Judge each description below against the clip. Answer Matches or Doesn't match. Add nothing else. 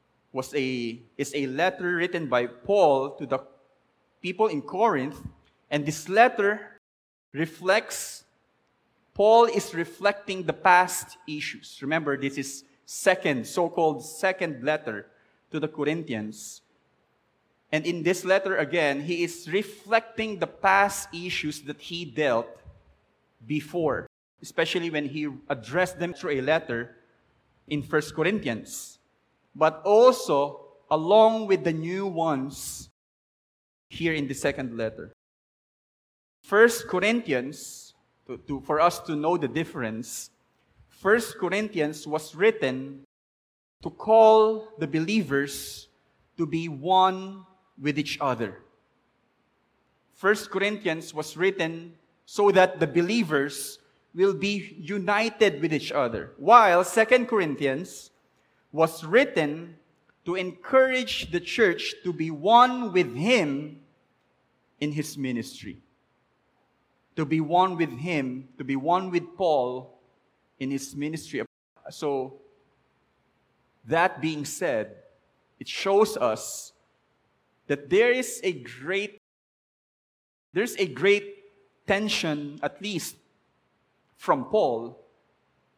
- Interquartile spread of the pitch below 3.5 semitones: Doesn't match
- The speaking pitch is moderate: Matches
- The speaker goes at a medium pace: Doesn't match